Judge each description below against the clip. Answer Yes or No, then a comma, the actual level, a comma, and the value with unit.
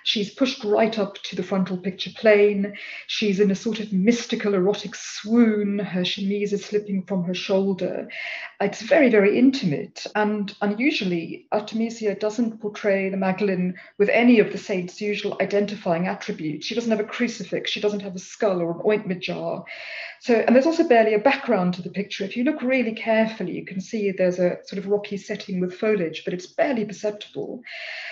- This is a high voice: Yes, high, 205 Hz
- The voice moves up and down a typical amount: No, narrow, 2.3 semitones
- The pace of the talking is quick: No, average, 185 wpm